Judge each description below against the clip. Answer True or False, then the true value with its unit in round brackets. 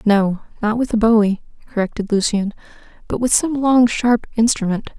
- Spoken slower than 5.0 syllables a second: False (5.1 syllables/s)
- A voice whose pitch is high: True (220 Hz)